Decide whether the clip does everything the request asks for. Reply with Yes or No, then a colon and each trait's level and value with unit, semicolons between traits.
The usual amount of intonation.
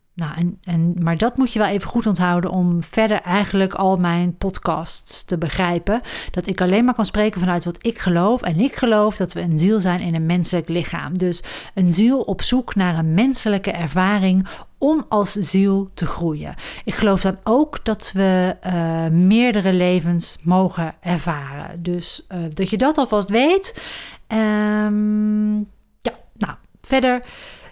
Yes: average, 3.4 semitones